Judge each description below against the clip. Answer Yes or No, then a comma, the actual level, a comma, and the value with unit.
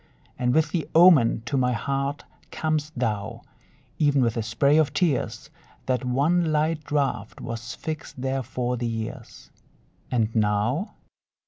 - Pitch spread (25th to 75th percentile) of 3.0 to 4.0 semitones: No, average, 4.7 semitones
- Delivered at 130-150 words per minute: Yes, average, 140 wpm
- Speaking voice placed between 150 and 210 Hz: No, low, 130 Hz